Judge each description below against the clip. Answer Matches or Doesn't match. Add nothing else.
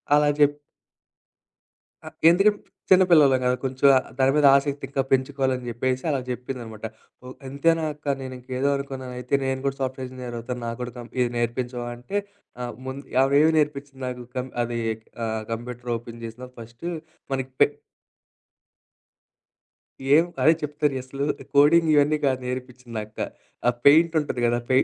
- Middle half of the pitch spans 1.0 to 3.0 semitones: Matches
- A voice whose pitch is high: Doesn't match